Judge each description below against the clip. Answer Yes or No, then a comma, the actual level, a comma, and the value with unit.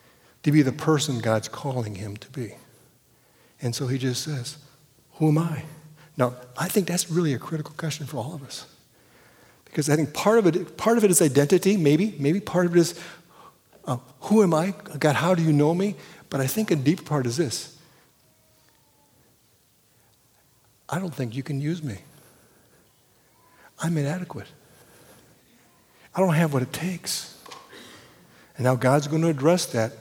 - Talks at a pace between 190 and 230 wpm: No, average, 170 wpm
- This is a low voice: No, medium, 150 Hz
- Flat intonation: No, average, 5.0 semitones